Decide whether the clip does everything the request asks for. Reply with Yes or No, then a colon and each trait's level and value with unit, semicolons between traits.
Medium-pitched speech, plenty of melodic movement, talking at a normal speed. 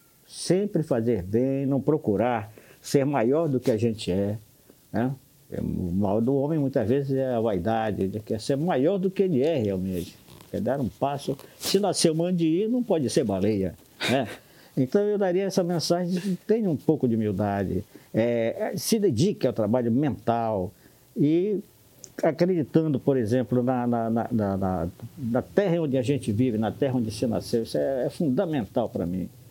No: low, 130 Hz; wide, 6.1 semitones; average, 170 wpm